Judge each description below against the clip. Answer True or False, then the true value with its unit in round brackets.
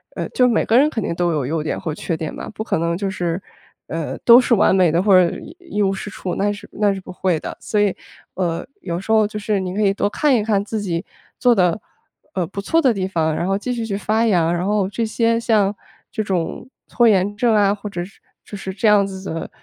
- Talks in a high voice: True (200 Hz)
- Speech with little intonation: False (3.3 semitones)